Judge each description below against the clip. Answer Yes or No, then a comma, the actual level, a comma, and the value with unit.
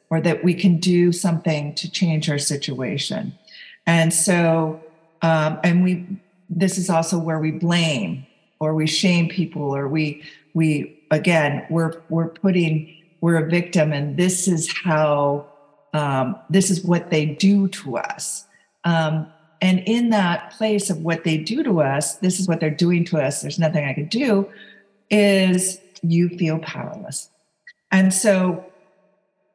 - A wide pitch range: No, average, 2.9 semitones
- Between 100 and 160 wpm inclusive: Yes, average, 155 wpm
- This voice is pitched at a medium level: Yes, medium, 170 Hz